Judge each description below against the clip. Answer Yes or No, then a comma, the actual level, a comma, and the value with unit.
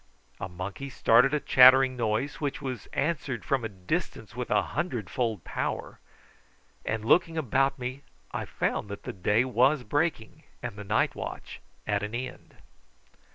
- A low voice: Yes, low, 125 Hz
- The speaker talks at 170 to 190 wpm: No, average, 155 wpm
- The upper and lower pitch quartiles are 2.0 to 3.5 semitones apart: No, average, 4.3 semitones